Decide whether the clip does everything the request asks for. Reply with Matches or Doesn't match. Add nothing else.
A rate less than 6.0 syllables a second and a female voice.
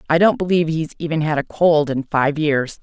Matches